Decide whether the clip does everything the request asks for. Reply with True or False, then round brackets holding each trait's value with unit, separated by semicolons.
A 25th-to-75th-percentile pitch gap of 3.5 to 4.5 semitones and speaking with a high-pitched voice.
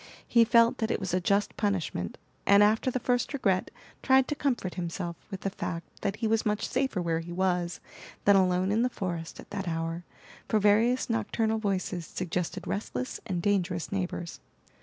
True (4.0 semitones; 200 Hz)